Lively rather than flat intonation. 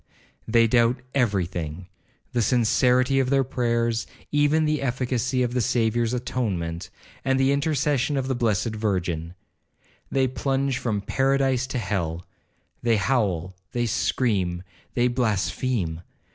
No: average, 4.6 semitones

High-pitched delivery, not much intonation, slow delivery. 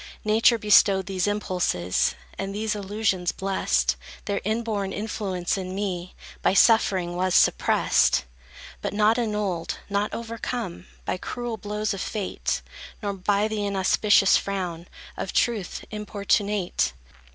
Yes: high, 200 Hz; narrow, 2.3 semitones; slow, 120 wpm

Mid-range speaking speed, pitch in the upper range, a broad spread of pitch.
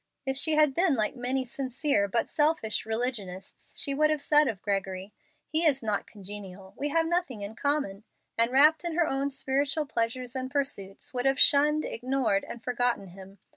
Yes: average, 180 wpm; very high, 260 Hz; wide, 5.8 semitones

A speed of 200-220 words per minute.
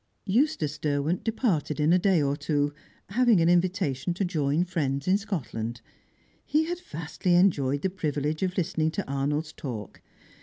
No: average, 155 wpm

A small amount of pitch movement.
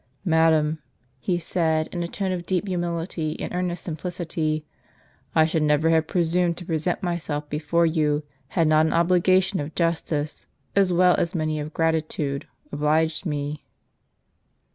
Yes: narrow, 2.1 semitones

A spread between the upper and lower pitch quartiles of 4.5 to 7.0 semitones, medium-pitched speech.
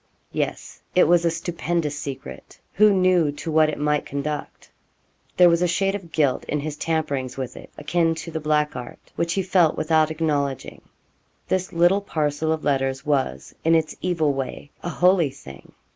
No: average, 2.9 semitones; medium, 155 Hz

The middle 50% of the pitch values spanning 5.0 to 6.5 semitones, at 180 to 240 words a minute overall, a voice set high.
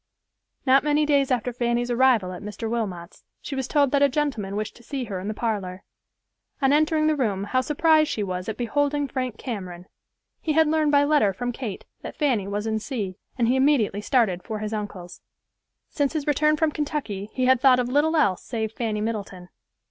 Yes: wide, 5.6 semitones; average, 200 wpm; high, 245 Hz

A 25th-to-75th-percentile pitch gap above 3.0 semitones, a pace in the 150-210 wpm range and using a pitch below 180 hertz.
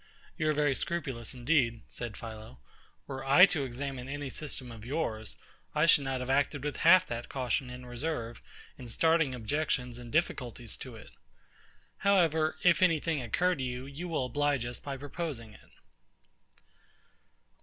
Yes: average, 4.2 semitones; average, 160 wpm; low, 135 Hz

